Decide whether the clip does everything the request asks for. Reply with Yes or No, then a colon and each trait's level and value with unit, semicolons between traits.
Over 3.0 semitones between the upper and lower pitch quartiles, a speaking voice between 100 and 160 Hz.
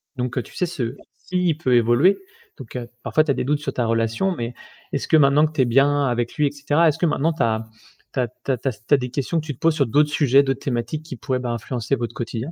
Yes: average, 3.9 semitones; low, 135 Hz